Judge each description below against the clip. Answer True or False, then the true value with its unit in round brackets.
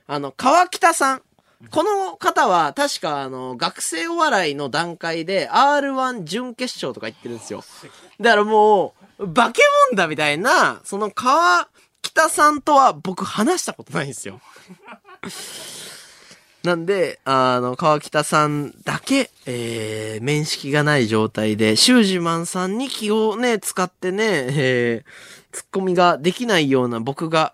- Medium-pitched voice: True (175 Hz)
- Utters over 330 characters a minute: False (270 characters per minute)